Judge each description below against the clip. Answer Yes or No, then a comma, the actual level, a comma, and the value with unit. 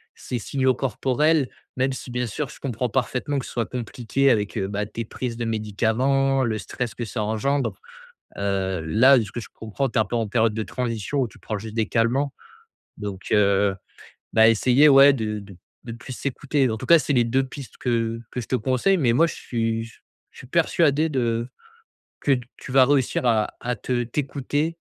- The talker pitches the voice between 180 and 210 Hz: No, low, 120 Hz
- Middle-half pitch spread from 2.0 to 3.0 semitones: No, average, 3.4 semitones